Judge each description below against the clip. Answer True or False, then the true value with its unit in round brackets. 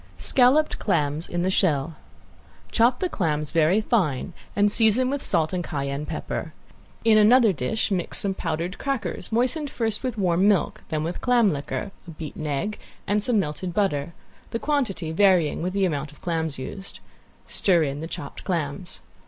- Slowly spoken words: False (165 wpm)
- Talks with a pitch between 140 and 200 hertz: True (185 Hz)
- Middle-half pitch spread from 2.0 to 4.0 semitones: False (5.6 semitones)